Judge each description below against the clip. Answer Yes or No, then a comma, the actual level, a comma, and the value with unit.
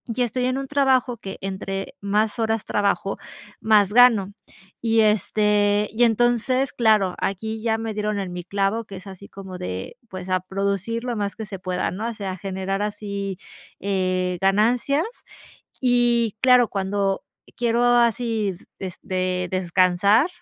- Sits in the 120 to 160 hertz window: No, high, 205 Hz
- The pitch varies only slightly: No, average, 3.2 semitones